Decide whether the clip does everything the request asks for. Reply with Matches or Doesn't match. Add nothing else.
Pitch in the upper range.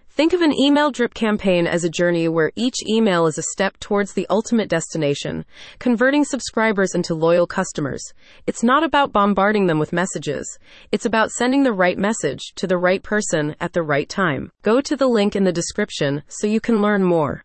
Matches